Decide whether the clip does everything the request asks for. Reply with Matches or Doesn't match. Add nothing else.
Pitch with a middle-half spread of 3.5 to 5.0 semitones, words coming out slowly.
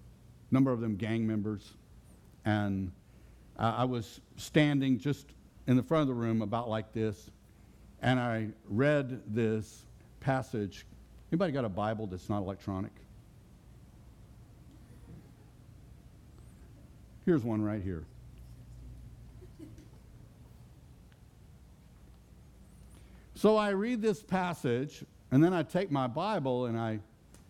Matches